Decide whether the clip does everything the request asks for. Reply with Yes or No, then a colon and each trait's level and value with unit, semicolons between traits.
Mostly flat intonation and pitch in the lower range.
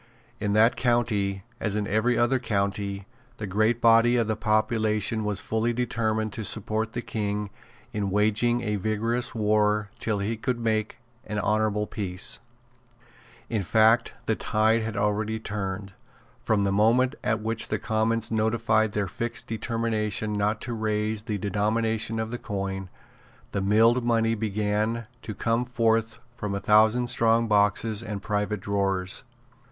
Yes: narrow, 1.7 semitones; low, 110 Hz